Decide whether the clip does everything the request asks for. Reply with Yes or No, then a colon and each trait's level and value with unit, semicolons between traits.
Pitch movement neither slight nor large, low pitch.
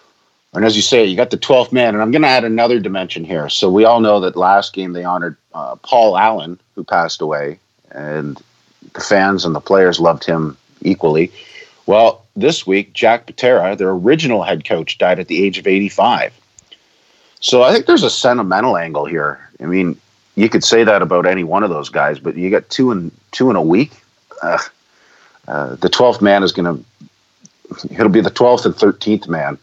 Yes: average, 4.0 semitones; very low, 95 Hz